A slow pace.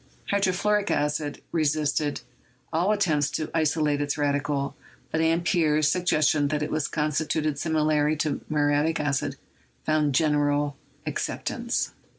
Yes: slow, 125 wpm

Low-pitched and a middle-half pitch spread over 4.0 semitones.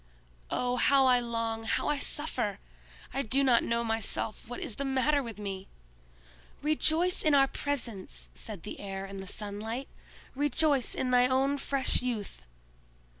No: very high, 250 Hz; average, 4.5 semitones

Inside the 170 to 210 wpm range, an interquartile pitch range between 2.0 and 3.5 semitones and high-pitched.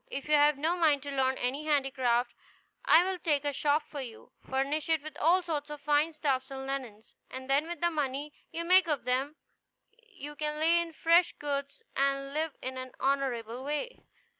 Yes: average, 195 wpm; average, 2.8 semitones; very high, 290 Hz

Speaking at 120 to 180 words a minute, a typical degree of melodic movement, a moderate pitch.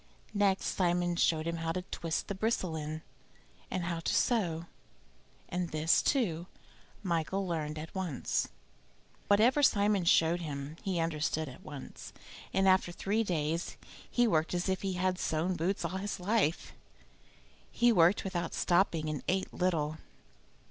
Yes: average, 150 wpm; average, 3.1 semitones; medium, 175 Hz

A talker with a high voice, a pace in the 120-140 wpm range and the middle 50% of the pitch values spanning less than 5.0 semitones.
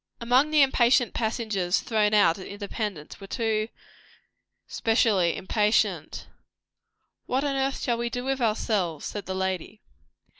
Yes: high, 220 Hz; slow, 135 wpm; average, 3.8 semitones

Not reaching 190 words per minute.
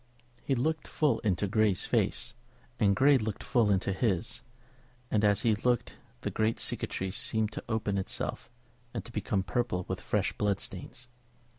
Yes: average, 160 wpm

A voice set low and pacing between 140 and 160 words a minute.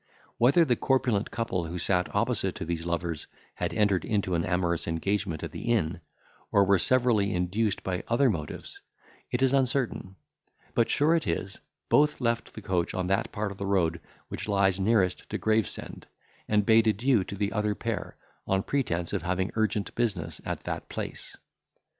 No: low, 100 Hz; average, 170 wpm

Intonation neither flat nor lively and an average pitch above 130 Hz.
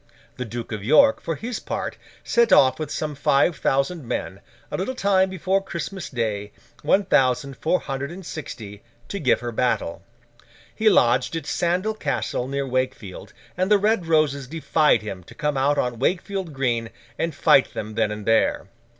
No: wide, 7.0 semitones; medium, 140 Hz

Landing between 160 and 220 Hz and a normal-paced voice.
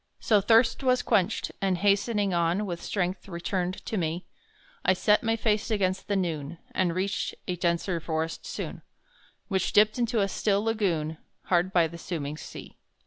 Yes: high, 190 Hz; average, 165 wpm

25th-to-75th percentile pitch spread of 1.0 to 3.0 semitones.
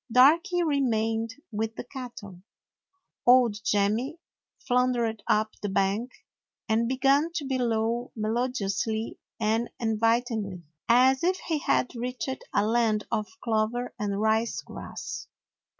Yes: average, 2.7 semitones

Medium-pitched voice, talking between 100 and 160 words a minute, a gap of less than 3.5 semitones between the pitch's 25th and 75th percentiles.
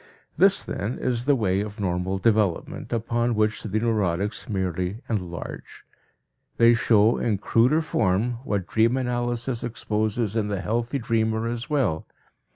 No: low, 110 Hz; average, 140 wpm; average, 3.0 semitones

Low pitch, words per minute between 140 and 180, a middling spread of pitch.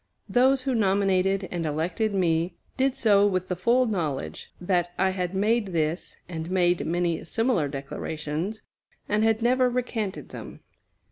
No: high, 190 Hz; average, 145 wpm; average, 4.4 semitones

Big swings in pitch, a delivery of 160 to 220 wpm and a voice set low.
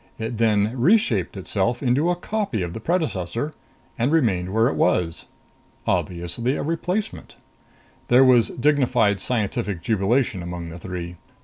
No: wide, 6.4 semitones; slow, 135 wpm; low, 115 Hz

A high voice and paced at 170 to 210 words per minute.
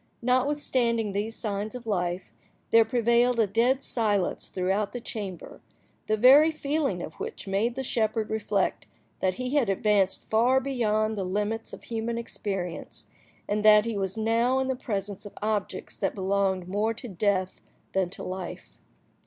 No: high, 215 Hz; average, 160 wpm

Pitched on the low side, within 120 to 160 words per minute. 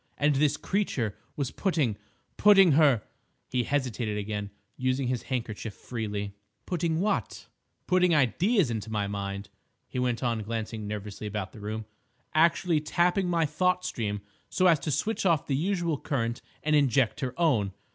Yes: low, 130 Hz; average, 150 wpm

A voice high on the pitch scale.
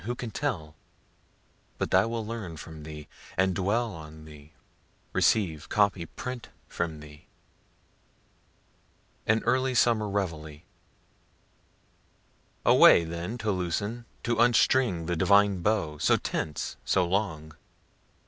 No: very low, 95 Hz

